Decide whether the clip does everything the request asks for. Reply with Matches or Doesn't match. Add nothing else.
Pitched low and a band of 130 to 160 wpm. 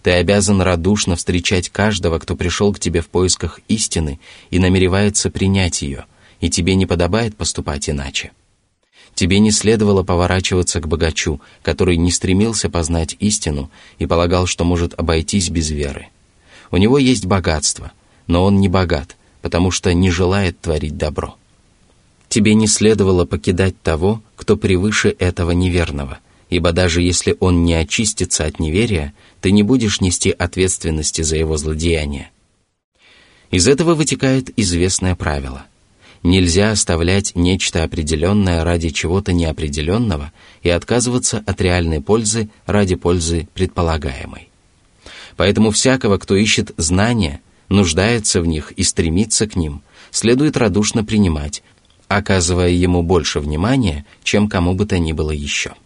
Matches